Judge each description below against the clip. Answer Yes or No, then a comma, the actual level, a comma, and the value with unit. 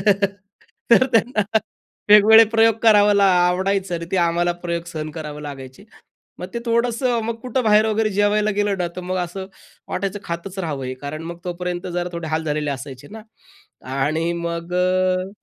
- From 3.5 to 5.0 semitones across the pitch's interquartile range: Yes, average, 3.9 semitones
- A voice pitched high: No, medium, 180 Hz